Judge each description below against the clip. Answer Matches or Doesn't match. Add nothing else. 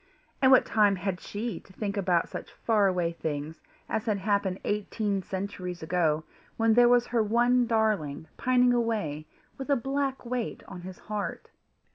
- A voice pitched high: Matches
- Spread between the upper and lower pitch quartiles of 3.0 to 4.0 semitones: Doesn't match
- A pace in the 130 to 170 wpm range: Matches